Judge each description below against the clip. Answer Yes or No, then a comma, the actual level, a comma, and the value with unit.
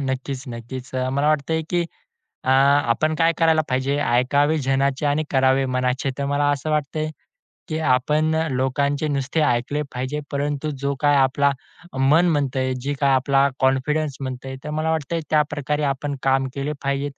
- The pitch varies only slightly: Yes, narrow, 2.1 semitones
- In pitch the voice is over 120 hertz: Yes, medium, 140 Hz